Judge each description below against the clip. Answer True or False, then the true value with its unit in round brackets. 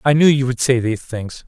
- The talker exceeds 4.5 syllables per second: True (5.8 syllables/s)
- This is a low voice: True (130 Hz)